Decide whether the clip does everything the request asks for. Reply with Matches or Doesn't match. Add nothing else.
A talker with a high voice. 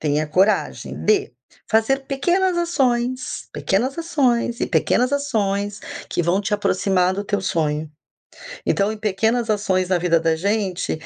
Matches